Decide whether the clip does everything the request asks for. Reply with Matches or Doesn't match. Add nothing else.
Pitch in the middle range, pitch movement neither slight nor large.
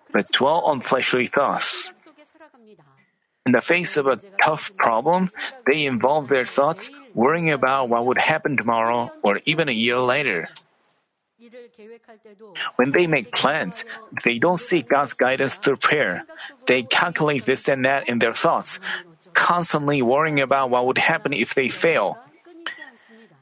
Doesn't match